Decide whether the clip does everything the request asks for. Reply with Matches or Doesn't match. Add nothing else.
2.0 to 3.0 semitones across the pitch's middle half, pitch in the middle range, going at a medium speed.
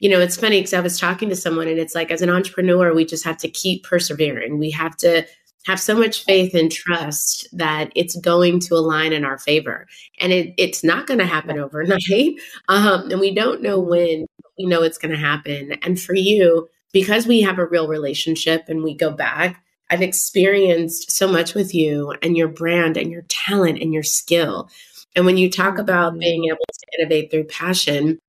Doesn't match